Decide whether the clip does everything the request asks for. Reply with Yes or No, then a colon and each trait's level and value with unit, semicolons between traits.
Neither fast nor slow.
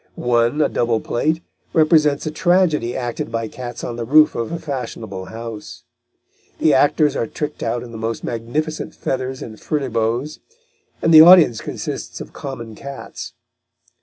Yes: average, 155 wpm